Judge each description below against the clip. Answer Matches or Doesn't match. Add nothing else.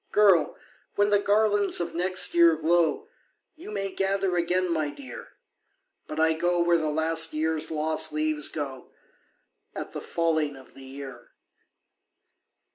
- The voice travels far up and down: Doesn't match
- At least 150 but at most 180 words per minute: Doesn't match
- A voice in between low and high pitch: Matches